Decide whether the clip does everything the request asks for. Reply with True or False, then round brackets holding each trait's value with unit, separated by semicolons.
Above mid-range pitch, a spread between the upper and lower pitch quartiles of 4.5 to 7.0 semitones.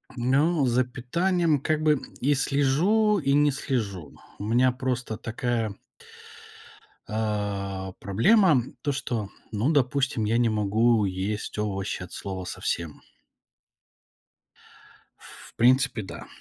False (120 Hz; 5.2 semitones)